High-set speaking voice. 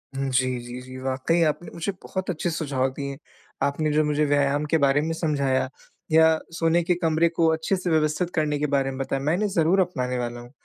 No: medium, 150 Hz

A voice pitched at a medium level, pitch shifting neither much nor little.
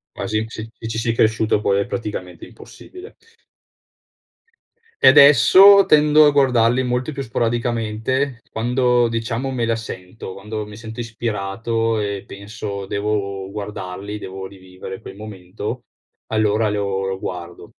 No: low, 110 Hz; average, 3.2 semitones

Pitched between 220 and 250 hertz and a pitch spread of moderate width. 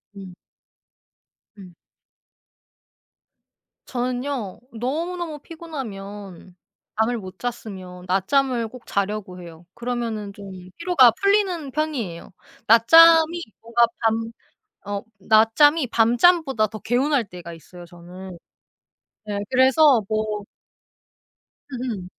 No: high, 230 Hz; wide, 5.9 semitones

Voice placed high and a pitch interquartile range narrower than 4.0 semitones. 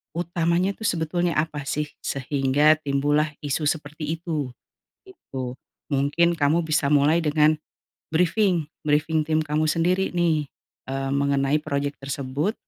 No: medium, 155 Hz; average, 2.8 semitones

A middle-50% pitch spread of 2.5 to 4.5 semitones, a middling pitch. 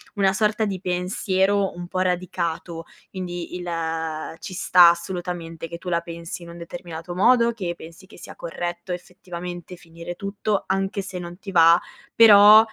No: narrow, 2.1 semitones; medium, 180 Hz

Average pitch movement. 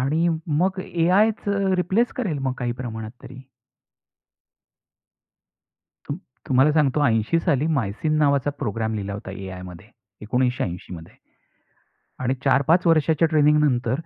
No: wide, 6.4 semitones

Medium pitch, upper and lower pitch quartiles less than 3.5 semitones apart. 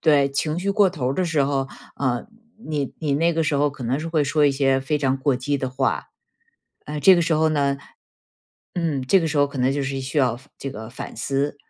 Yes: medium, 145 Hz; narrow, 2.6 semitones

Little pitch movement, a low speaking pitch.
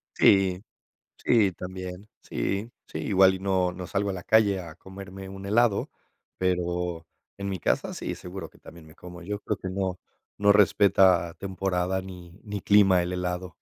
Yes: narrow, 1.7 semitones; very low, 95 Hz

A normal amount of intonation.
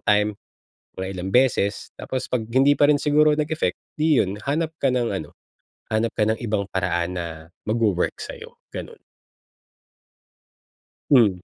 No: wide, 6.6 semitones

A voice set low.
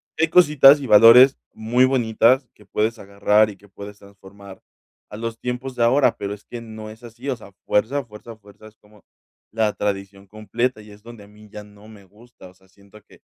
Yes: low, 110 Hz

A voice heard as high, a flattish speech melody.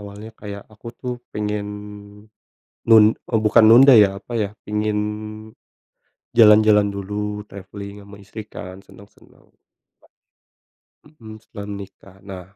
No: low, 105 Hz; narrow, 1.3 semitones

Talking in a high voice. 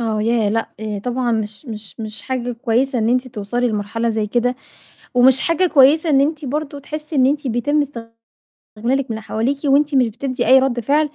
Yes: very high, 250 Hz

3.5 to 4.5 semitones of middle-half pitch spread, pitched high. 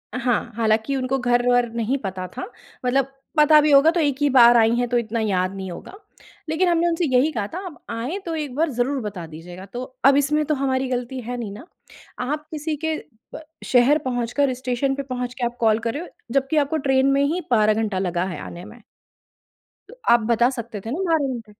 Yes: average, 3.9 semitones; very high, 250 Hz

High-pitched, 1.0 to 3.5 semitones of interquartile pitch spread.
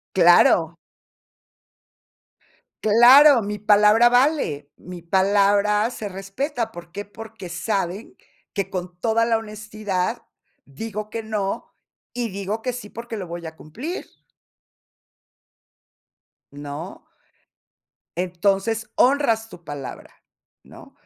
No: high, 210 Hz; average, 3.9 semitones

